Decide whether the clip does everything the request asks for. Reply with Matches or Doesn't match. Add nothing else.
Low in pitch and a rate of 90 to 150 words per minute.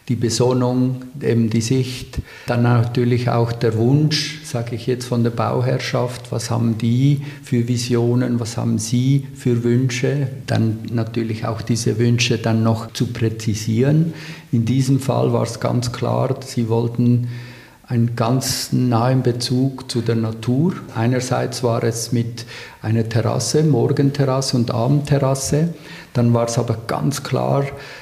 Matches